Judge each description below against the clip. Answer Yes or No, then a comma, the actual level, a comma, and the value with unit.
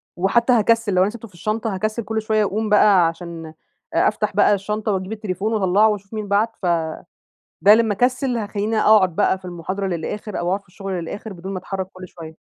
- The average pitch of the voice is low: No, high, 200 Hz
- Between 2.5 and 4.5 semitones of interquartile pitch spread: Yes, average, 2.8 semitones